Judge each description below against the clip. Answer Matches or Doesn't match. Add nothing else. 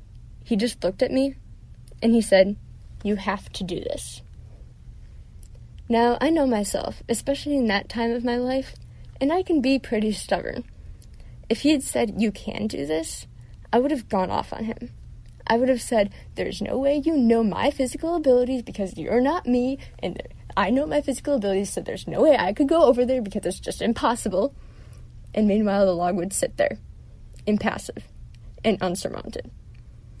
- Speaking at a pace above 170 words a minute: Matches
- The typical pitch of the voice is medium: Doesn't match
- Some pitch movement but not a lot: Matches